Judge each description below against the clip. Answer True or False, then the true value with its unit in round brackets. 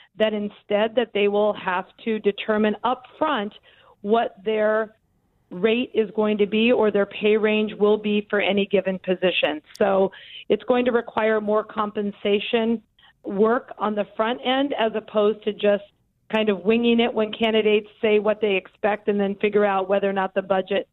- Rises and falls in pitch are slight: True (1.5 semitones)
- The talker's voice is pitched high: True (215 Hz)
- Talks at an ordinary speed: True (180 wpm)